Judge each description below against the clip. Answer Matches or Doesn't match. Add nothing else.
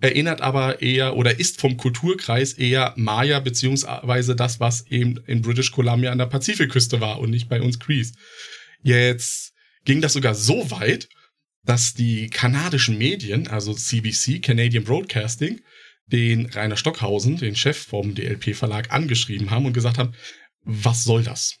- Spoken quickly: Doesn't match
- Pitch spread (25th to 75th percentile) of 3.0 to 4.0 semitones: Doesn't match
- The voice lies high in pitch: Doesn't match